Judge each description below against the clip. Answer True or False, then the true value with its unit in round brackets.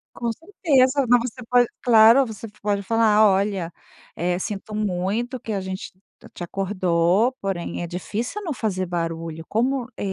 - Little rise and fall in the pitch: False (4.6 semitones)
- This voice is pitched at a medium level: False (210 Hz)